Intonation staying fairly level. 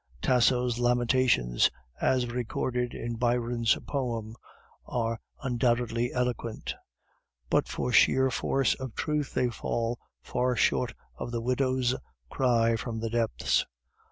Yes: narrow, 1.5 semitones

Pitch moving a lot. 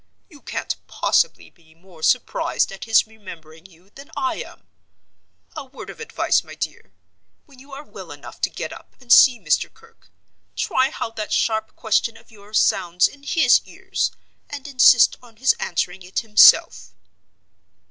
Yes: wide, 6.4 semitones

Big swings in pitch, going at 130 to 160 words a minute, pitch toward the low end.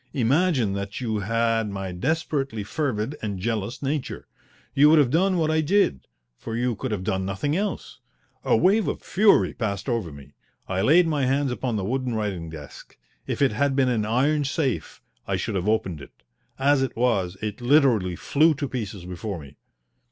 No: wide, 6.2 semitones; average, 185 wpm; low, 120 Hz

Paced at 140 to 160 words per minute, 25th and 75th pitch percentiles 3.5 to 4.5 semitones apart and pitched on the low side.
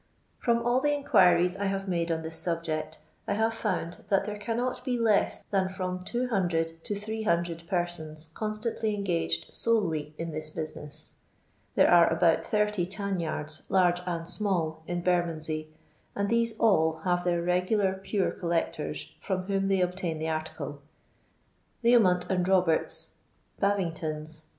No: average, 145 wpm; average, 3.8 semitones; medium, 180 Hz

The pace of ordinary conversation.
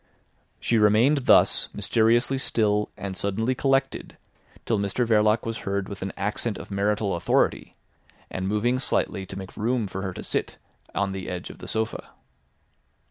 Yes: average, 160 wpm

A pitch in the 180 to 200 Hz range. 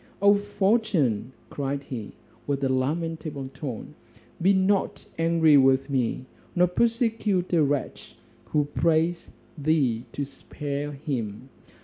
No: medium, 150 Hz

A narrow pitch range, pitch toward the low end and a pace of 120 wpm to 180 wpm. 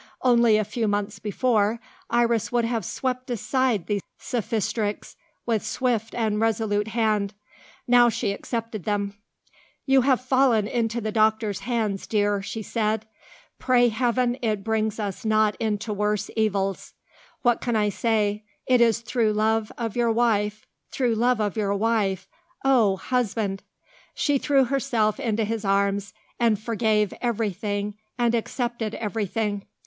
No: narrow, 2.3 semitones; high, 220 Hz; average, 140 wpm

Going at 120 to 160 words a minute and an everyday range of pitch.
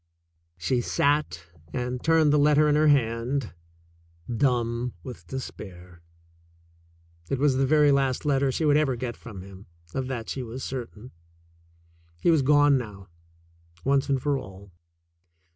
Yes: average, 145 wpm; average, 3.8 semitones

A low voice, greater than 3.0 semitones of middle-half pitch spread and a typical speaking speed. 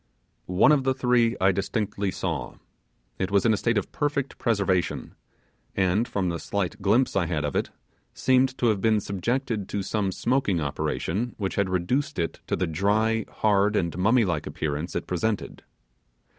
Yes: low, 100 Hz; average, 4.1 semitones; average, 170 wpm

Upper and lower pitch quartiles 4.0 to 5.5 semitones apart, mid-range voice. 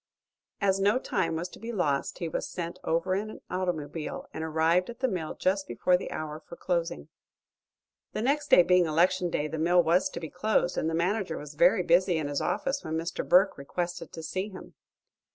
No: average, 2.8 semitones; medium, 175 Hz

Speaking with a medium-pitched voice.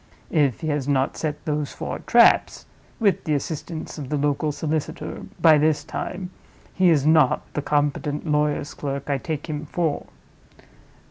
Yes: medium, 150 Hz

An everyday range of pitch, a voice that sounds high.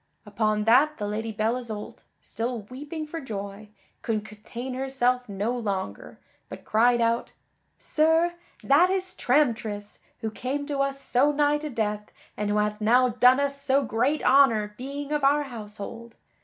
Yes: average, 4.7 semitones; high, 245 Hz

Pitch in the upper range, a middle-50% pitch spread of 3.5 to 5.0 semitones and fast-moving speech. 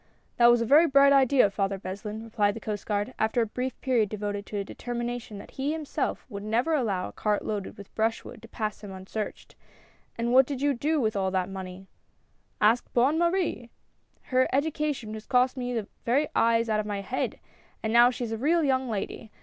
Yes: high, 230 Hz; average, 3.9 semitones; fast, 220 wpm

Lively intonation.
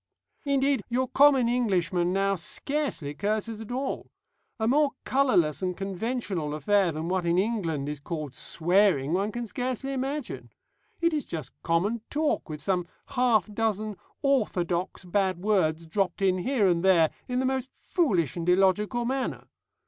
Yes: wide, 6.3 semitones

